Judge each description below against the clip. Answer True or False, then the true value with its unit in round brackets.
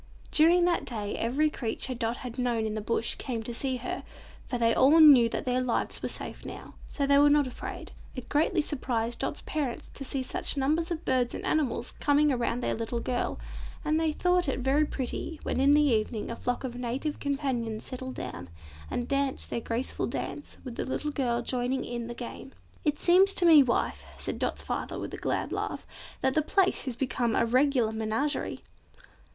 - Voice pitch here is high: True (260 Hz)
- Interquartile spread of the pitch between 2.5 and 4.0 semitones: True (3.7 semitones)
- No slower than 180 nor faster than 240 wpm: True (200 wpm)